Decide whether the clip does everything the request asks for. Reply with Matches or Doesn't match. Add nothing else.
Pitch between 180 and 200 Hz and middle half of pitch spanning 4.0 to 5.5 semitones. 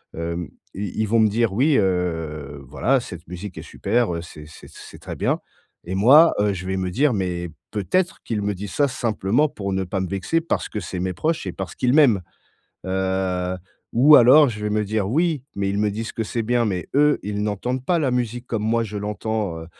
Doesn't match